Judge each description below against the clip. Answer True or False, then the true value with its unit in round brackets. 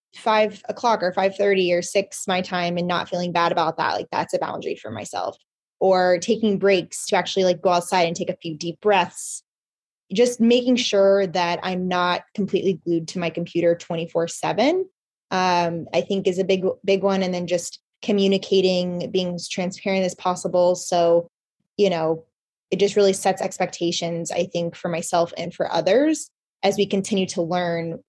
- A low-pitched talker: False (185 Hz)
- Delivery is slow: False (185 wpm)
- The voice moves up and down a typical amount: False (2.2 semitones)